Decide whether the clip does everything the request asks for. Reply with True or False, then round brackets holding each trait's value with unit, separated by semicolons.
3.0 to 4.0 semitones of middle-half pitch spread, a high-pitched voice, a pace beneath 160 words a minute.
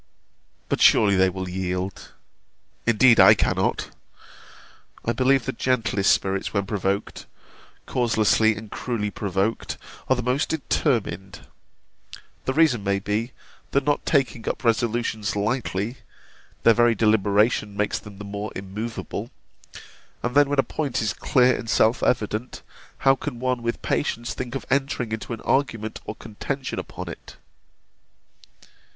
False (3.7 semitones; 115 Hz; 135 wpm)